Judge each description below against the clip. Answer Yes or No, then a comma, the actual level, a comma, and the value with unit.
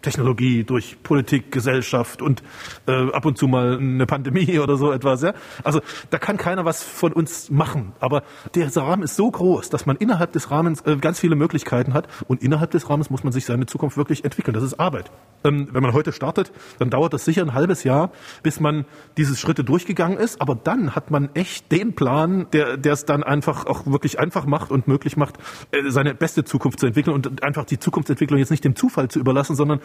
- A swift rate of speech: Yes, fast, 215 wpm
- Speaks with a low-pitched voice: No, medium, 145 Hz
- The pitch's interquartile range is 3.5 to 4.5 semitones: No, average, 3.0 semitones